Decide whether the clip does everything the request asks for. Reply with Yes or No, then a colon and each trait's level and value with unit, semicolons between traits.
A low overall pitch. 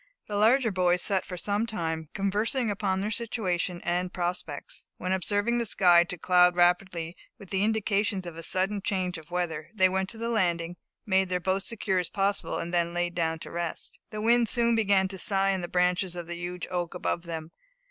No: medium, 185 Hz